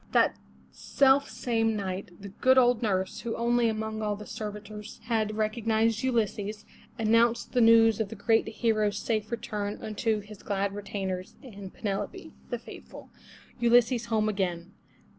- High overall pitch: Yes, high, 215 Hz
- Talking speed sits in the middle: Yes, average, 145 wpm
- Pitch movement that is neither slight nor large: No, narrow, 1.9 semitones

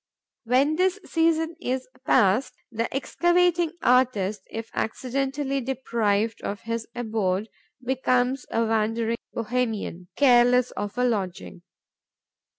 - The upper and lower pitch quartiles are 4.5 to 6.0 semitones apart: No, average, 3.3 semitones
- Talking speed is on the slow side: Yes, slow, 105 wpm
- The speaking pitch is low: No, high, 245 Hz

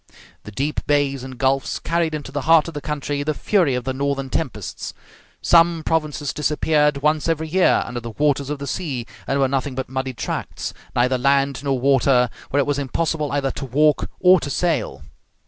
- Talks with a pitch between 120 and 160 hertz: Yes, medium, 140 Hz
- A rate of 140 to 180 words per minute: No, average, 195 wpm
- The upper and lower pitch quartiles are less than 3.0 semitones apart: Yes, narrow, 2.5 semitones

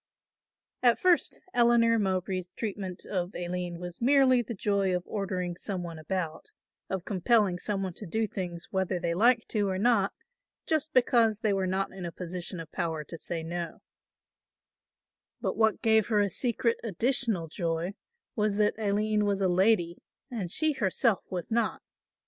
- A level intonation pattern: No, average, 3.9 semitones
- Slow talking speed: No, average, 165 wpm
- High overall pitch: Yes, high, 195 Hz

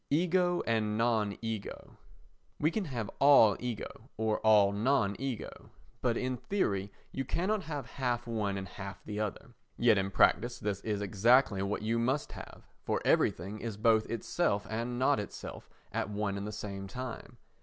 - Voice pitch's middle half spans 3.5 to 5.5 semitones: Yes, average, 3.9 semitones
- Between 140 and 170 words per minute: Yes, average, 165 wpm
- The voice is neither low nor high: No, low, 110 Hz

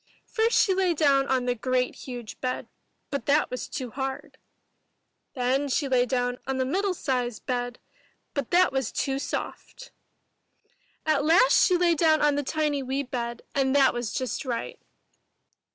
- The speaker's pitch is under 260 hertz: No, very high, 270 Hz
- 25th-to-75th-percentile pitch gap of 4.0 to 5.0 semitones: No, average, 3.4 semitones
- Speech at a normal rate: Yes, average, 165 wpm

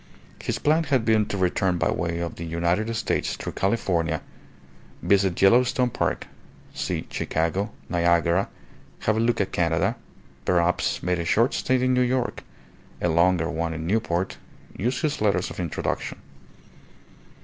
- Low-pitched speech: Yes, very low, 95 Hz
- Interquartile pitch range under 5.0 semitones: No, average, 5.3 semitones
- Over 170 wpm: No, average, 150 wpm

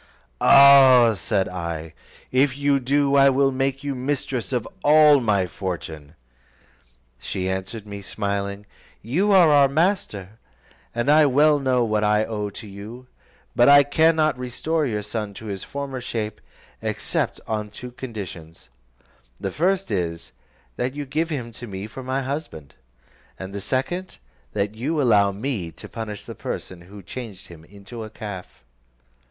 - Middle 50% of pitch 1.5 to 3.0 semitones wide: No, wide, 5.6 semitones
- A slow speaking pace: No, average, 155 wpm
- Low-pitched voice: Yes, low, 115 Hz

